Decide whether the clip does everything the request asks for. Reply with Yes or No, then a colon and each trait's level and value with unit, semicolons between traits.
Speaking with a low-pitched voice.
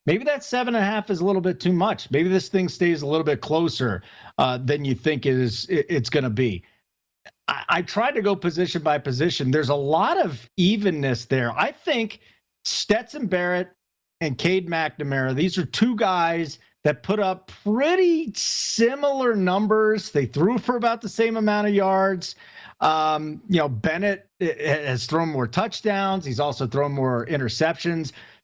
No: medium, 170 Hz